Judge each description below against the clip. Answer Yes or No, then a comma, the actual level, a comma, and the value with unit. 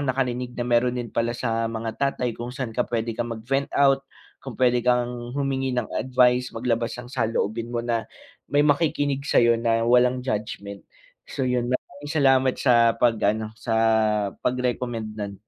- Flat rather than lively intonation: Yes, narrow, 2.1 semitones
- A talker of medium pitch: No, low, 125 Hz